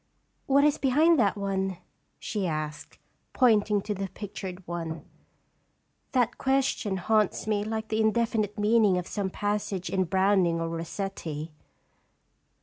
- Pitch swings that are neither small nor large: Yes, average, 3.1 semitones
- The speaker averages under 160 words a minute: Yes, slow, 135 wpm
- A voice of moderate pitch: No, high, 205 Hz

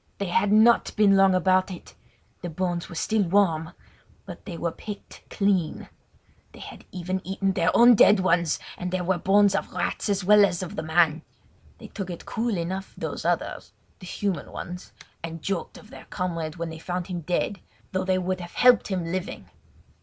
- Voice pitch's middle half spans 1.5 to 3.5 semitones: Yes, narrow, 2.5 semitones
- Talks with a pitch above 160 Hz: Yes, medium, 185 Hz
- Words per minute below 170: No, average, 185 wpm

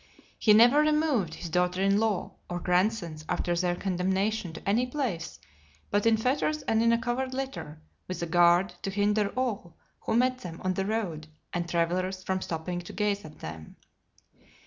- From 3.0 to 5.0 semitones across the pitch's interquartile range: Yes, average, 4.5 semitones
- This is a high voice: Yes, high, 195 Hz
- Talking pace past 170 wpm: Yes, average, 180 wpm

